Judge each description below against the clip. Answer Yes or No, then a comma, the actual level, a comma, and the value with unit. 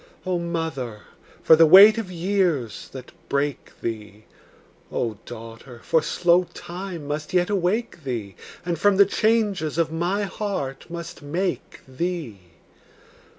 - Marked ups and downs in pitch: Yes, wide, 5.8 semitones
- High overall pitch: No, medium, 165 Hz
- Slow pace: Yes, slow, 130 wpm